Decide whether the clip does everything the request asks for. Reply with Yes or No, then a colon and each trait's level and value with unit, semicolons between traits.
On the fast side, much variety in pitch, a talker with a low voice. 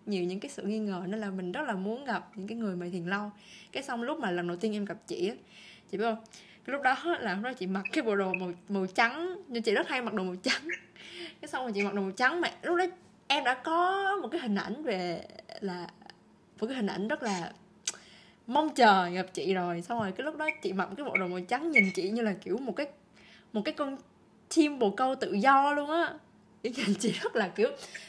No: fast, 255 wpm; wide, 6.0 semitones; high, 215 Hz